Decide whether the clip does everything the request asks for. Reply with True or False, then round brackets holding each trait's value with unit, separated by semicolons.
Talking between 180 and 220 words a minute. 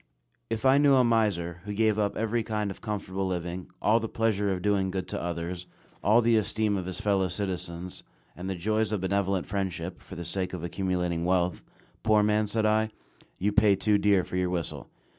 True (200 wpm)